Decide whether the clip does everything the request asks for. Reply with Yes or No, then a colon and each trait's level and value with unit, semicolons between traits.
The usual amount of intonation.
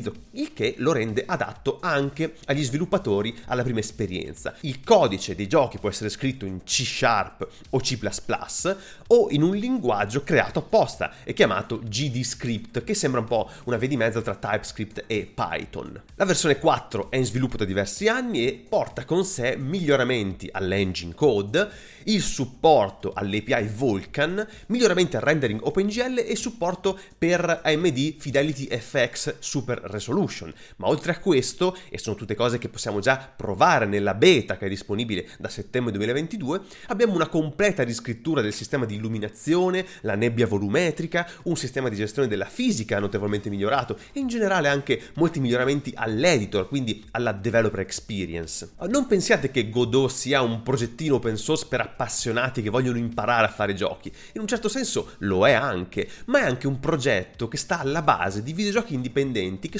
No: wide, 7.1 semitones